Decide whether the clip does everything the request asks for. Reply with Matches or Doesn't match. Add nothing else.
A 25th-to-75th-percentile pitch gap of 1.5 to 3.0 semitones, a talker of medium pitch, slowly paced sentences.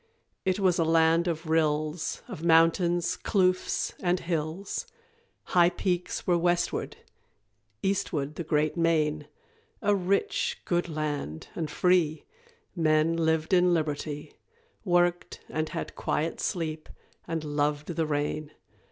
Matches